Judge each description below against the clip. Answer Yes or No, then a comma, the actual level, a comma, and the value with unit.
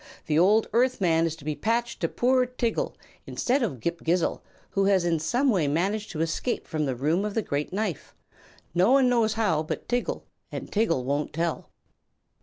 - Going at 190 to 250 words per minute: Yes, average, 195 wpm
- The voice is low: No, high, 190 Hz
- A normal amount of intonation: No, wide, 6.4 semitones